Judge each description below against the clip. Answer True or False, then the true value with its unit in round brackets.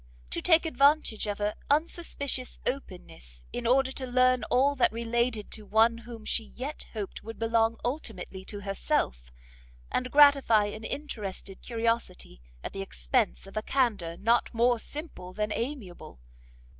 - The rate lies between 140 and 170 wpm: True (145 wpm)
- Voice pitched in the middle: False (230 Hz)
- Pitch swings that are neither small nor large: True (4.1 semitones)